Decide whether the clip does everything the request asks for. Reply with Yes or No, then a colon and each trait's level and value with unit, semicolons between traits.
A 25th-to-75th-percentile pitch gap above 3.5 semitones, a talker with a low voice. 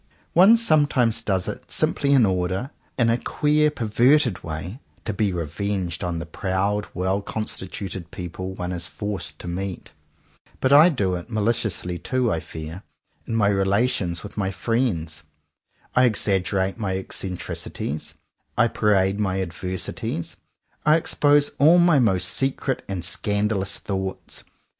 Yes: average, 4.5 semitones; low, 100 Hz